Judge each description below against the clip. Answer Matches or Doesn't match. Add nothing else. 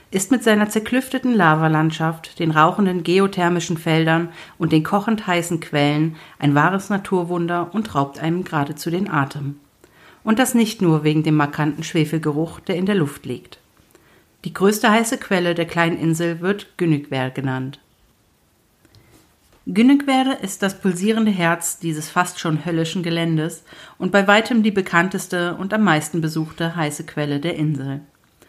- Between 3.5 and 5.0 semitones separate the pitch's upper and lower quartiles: Matches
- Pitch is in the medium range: Matches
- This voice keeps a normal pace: Matches